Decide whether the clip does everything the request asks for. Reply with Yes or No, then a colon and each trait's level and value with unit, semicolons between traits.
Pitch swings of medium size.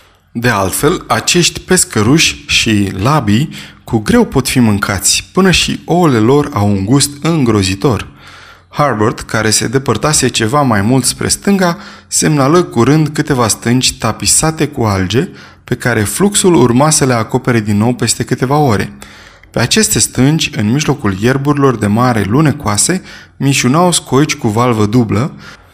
No: wide, 5.7 semitones